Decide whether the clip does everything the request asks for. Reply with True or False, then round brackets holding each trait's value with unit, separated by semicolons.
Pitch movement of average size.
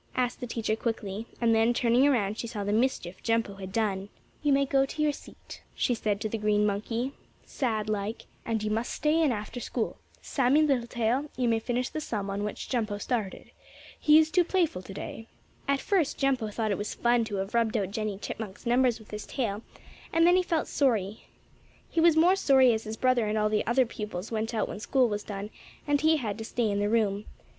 True (3.8 semitones)